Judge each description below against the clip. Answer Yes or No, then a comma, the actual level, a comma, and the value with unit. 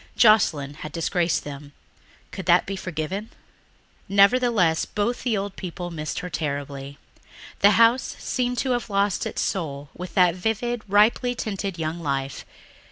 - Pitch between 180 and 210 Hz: Yes, medium, 185 Hz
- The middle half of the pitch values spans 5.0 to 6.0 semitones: Yes, wide, 5.6 semitones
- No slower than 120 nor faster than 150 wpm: Yes, average, 145 wpm